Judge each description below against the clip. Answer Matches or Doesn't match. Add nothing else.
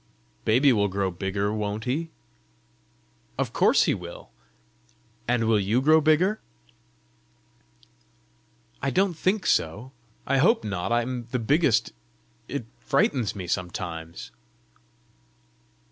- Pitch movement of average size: Doesn't match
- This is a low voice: Matches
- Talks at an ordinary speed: Doesn't match